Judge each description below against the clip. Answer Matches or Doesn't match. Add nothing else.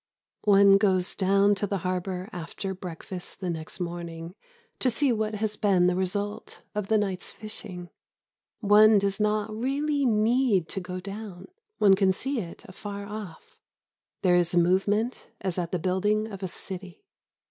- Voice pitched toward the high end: Matches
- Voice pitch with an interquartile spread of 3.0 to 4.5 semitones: Doesn't match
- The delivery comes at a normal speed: Matches